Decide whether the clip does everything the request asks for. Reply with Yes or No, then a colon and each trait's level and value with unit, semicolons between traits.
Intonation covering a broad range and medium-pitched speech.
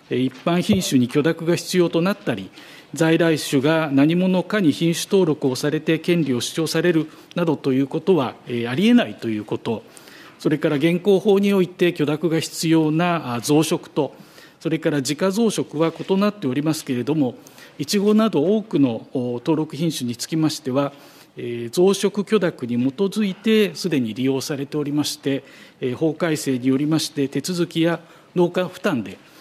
No: average, 4.1 semitones; medium, 160 Hz